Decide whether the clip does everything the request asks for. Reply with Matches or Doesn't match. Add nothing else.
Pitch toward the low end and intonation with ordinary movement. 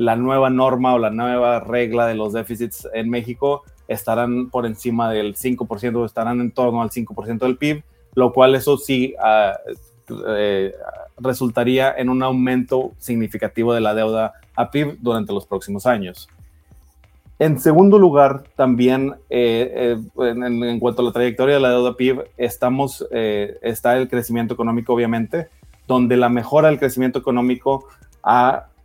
Doesn't match